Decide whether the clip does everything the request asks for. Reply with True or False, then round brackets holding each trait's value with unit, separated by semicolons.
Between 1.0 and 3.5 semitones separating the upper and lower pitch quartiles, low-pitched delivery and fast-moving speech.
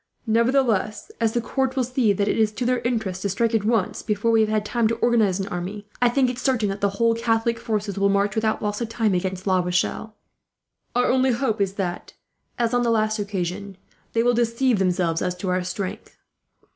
False (3.0 semitones; 215 Hz; 220 wpm)